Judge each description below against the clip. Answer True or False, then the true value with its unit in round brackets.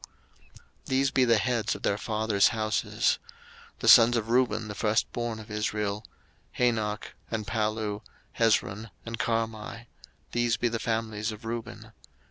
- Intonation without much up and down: True (1.7 semitones)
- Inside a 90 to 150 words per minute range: True (140 wpm)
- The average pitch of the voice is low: True (115 Hz)